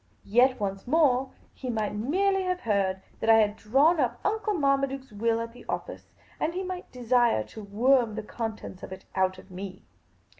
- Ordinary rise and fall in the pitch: Yes, average, 4.9 semitones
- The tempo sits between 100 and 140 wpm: No, average, 185 wpm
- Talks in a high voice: Yes, high, 235 Hz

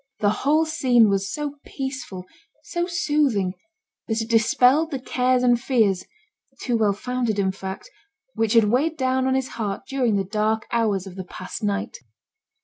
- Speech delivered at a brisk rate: No, average, 165 wpm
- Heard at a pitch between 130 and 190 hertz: No, high, 230 Hz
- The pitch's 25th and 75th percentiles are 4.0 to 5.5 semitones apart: Yes, average, 4.5 semitones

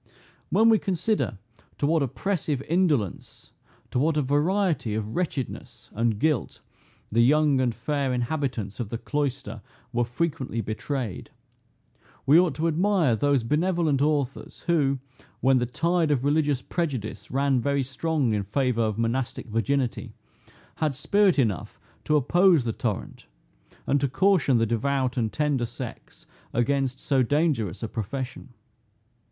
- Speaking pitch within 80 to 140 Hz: Yes, low, 135 Hz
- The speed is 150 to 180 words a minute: No, average, 140 wpm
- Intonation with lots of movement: No, average, 4.5 semitones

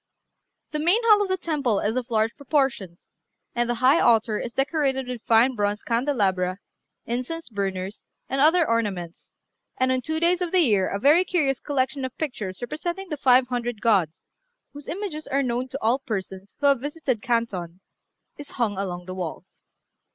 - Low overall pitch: No, very high, 250 Hz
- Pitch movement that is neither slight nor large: No, wide, 5.7 semitones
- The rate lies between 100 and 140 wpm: No, average, 175 wpm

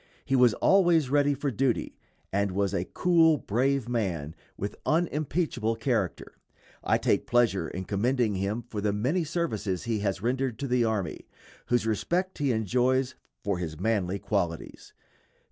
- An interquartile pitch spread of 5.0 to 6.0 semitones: Yes, wide, 5.5 semitones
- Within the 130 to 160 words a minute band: Yes, average, 150 wpm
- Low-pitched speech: Yes, low, 115 Hz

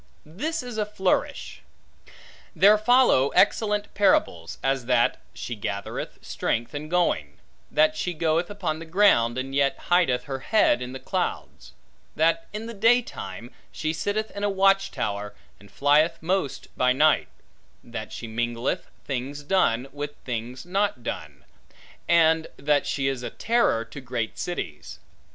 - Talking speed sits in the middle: Yes, average, 145 wpm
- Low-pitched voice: No, medium, 150 Hz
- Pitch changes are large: Yes, wide, 7.8 semitones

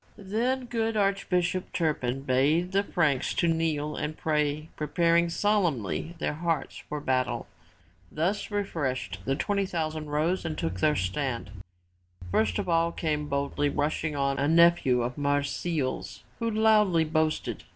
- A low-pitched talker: No, medium, 155 Hz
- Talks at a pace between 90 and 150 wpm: Yes, average, 140 wpm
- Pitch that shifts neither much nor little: Yes, average, 4.0 semitones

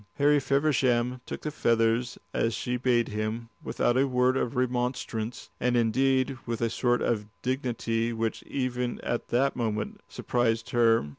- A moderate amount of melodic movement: No, narrow, 1.9 semitones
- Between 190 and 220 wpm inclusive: No, average, 150 wpm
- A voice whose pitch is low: Yes, low, 120 Hz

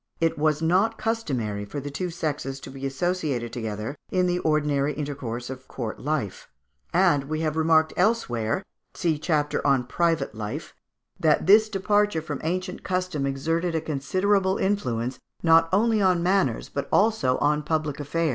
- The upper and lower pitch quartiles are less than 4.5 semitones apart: No, average, 5.0 semitones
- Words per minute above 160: No, average, 155 wpm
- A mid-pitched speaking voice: Yes, medium, 155 Hz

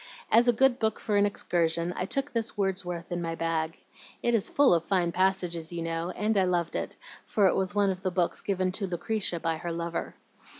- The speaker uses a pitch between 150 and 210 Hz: Yes, medium, 185 Hz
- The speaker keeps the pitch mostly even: No, average, 3.3 semitones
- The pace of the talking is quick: Yes, fast, 220 wpm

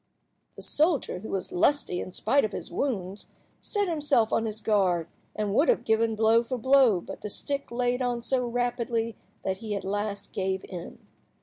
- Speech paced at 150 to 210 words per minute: Yes, average, 185 wpm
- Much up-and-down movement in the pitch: No, average, 4.3 semitones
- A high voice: Yes, high, 225 Hz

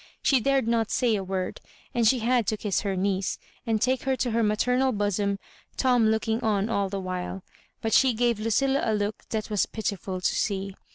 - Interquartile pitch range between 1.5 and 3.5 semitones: Yes, average, 3.2 semitones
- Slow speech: No, fast, 205 wpm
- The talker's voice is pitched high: Yes, high, 220 Hz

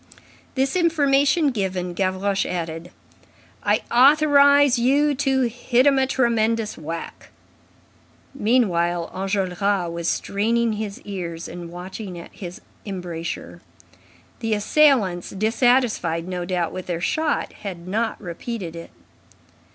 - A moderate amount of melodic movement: No, wide, 6.4 semitones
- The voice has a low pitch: No, high, 205 Hz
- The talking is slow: Yes, slow, 110 wpm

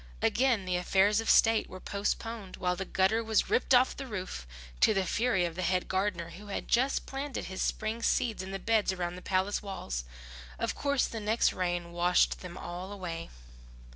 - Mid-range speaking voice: No, high, 195 Hz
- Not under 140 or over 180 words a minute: No, average, 195 wpm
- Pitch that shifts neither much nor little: Yes, average, 3.7 semitones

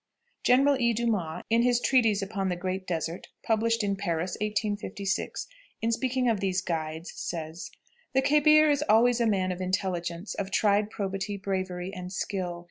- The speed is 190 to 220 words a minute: No, average, 160 wpm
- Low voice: No, high, 200 Hz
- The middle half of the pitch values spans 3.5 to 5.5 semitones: Yes, average, 4.0 semitones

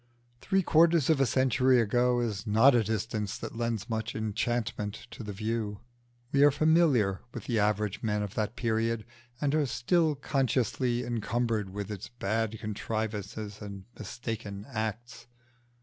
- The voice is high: No, low, 115 Hz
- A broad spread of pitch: No, average, 3.0 semitones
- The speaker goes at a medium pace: Yes, average, 150 wpm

